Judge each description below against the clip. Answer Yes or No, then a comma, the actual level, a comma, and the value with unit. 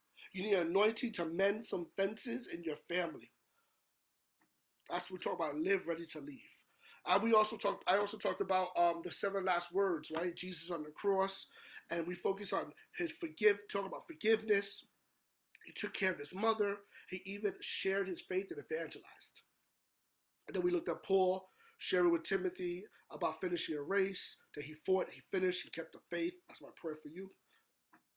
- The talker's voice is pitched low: No, high, 190 Hz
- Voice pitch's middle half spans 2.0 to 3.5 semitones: Yes, average, 2.8 semitones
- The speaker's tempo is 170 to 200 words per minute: Yes, average, 185 wpm